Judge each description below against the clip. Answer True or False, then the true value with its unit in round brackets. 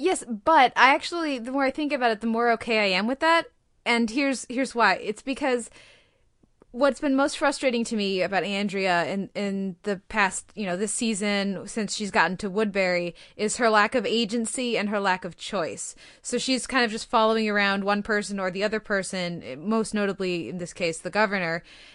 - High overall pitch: True (220 Hz)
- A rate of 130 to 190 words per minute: False (200 wpm)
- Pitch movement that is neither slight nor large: True (3.8 semitones)